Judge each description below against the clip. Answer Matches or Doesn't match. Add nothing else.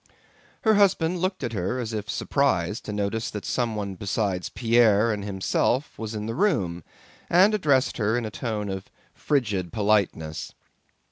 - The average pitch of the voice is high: Doesn't match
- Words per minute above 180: Doesn't match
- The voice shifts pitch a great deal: Doesn't match